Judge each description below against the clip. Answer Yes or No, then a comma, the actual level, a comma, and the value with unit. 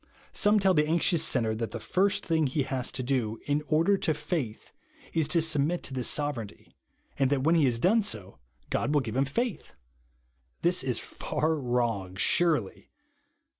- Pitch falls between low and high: Yes, medium, 145 Hz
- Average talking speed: Yes, average, 175 wpm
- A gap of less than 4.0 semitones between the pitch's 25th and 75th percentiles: No, average, 5.3 semitones